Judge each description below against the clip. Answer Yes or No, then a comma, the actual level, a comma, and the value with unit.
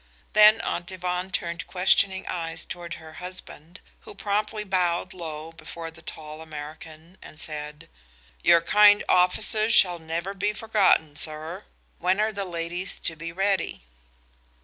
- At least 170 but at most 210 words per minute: No, average, 140 wpm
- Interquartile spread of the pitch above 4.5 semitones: No, average, 3.0 semitones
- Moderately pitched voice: Yes, medium, 175 Hz